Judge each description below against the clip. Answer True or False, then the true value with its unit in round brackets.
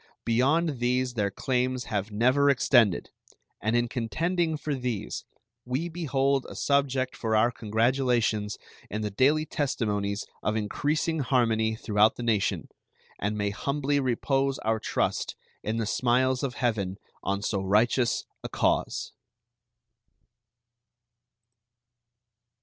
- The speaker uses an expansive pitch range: False (4.0 semitones)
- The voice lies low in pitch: True (120 Hz)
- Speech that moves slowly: True (120 wpm)